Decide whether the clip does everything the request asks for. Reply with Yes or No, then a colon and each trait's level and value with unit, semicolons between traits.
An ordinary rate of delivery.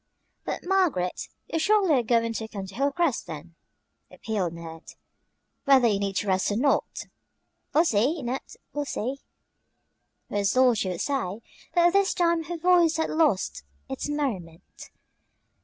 Yes: average, 145 wpm